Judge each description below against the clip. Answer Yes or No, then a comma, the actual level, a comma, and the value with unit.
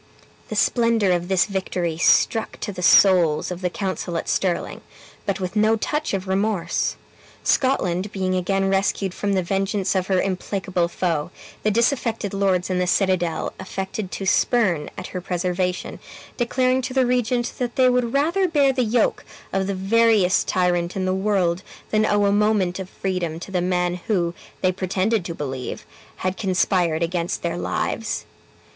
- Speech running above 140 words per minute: Yes, average, 165 wpm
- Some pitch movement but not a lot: Yes, average, 3.1 semitones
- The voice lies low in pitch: No, high, 190 Hz